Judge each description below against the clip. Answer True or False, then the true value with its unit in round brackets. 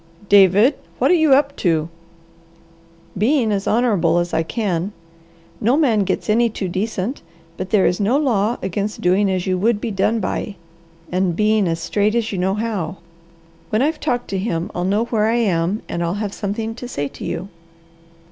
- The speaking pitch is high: True (205 Hz)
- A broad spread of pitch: False (3.8 semitones)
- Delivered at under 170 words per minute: False (185 wpm)